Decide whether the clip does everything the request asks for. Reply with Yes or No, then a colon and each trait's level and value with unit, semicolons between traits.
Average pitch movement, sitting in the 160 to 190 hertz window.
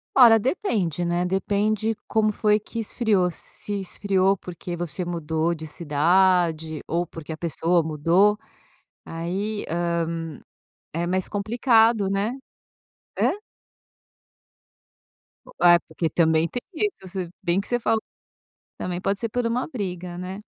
Yes: average, 3.7 semitones; medium, 185 Hz